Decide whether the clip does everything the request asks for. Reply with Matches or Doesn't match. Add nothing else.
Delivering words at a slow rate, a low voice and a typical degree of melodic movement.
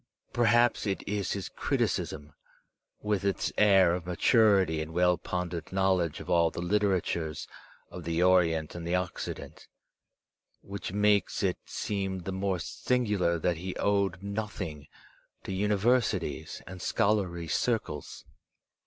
Matches